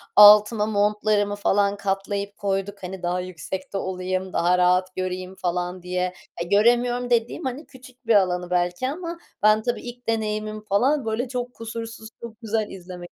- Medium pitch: No, high, 205 Hz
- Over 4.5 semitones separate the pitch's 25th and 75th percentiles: No, average, 3.7 semitones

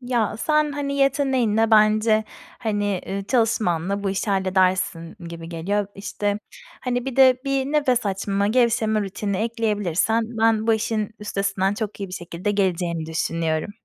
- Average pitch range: Yes, average, 3.4 semitones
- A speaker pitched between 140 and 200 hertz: No, high, 210 Hz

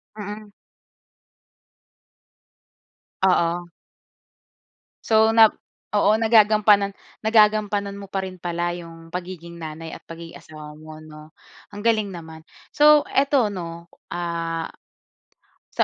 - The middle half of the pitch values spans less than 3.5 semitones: No, average, 4.2 semitones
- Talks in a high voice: No, medium, 180 Hz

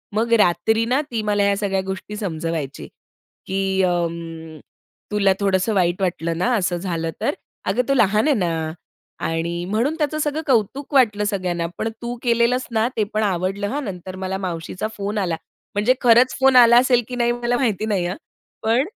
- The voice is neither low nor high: No, high, 205 Hz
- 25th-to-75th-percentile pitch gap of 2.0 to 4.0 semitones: No, average, 4.7 semitones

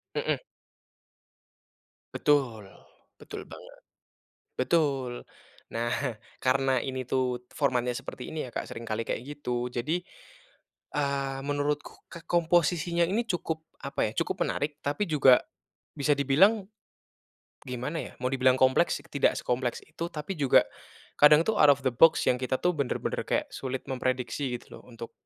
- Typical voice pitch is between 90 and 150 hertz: Yes, medium, 140 Hz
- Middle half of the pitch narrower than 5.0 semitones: Yes, average, 3.1 semitones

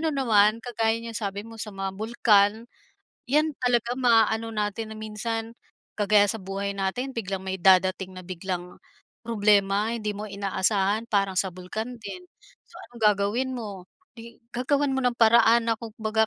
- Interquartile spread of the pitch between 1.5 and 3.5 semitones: Yes, average, 2.9 semitones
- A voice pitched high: Yes, high, 215 Hz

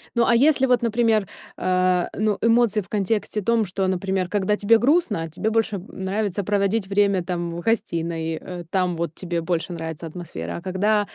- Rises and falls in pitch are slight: No, average, 3.7 semitones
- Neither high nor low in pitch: No, high, 195 Hz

